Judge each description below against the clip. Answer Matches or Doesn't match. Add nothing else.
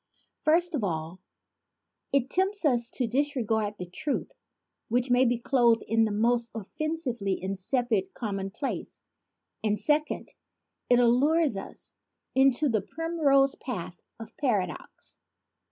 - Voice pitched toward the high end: Matches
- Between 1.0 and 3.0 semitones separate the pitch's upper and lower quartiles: Doesn't match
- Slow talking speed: Matches